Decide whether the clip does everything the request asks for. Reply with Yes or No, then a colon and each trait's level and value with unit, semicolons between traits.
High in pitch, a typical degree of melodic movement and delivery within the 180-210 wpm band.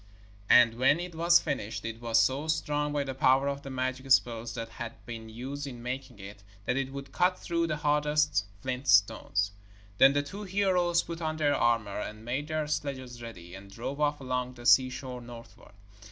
No: low, 130 Hz; average, 4.1 semitones; average, 195 wpm